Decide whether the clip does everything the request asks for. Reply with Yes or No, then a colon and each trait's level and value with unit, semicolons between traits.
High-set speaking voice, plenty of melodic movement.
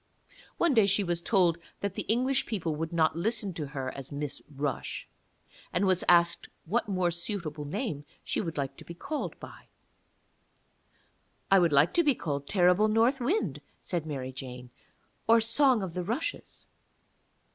No: medium, 175 Hz; wide, 6.5 semitones